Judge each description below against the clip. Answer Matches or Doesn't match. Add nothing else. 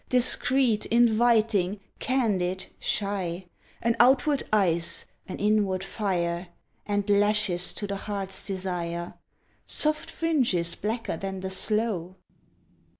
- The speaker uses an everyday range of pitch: Matches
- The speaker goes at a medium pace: Doesn't match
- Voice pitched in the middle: Doesn't match